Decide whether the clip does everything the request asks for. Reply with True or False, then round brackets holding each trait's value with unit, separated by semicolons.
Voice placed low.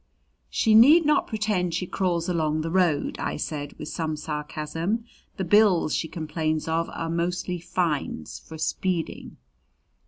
False (170 Hz)